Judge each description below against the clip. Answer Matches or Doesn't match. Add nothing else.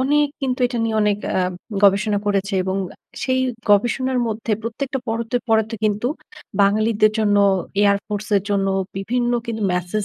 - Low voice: Doesn't match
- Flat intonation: Doesn't match